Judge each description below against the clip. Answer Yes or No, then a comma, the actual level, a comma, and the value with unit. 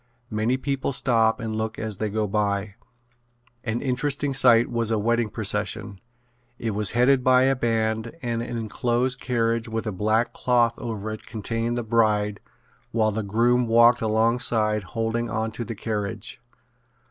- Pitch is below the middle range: Yes, low, 115 Hz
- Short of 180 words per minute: Yes, average, 160 wpm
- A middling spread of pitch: No, narrow, 1.8 semitones